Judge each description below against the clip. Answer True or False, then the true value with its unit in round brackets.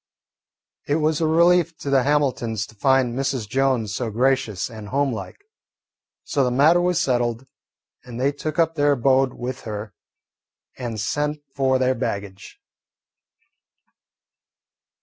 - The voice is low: True (130 Hz)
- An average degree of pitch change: True (3.8 semitones)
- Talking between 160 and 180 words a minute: False (135 wpm)